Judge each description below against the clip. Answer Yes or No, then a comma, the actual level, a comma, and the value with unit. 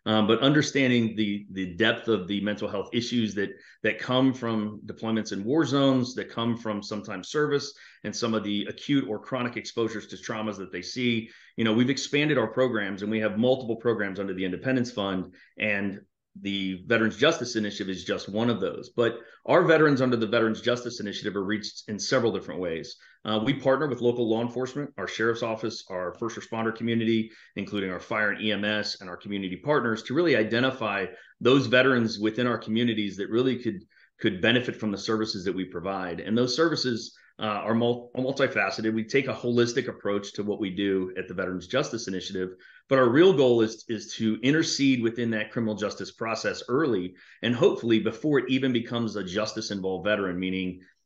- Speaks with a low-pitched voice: Yes, low, 110 Hz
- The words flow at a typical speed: Yes, average, 195 wpm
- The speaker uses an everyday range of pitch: Yes, average, 3.0 semitones